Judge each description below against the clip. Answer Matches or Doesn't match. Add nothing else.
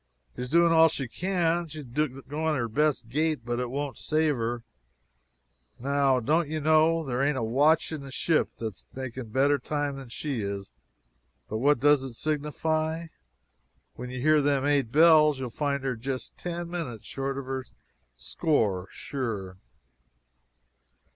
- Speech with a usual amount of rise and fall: Matches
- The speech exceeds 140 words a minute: Matches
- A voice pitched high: Doesn't match